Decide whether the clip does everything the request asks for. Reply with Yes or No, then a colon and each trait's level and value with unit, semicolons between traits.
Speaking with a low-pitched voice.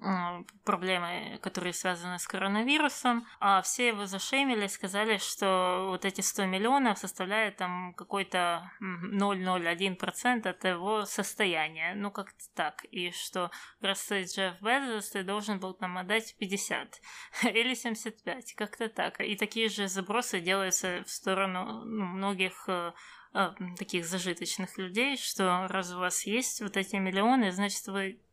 No: high, 195 Hz